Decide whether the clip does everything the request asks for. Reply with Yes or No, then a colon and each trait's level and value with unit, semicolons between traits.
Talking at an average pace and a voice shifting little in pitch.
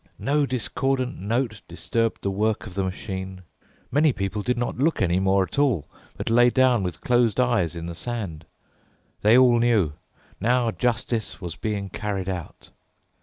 No: average, 165 wpm; average, 4.4 semitones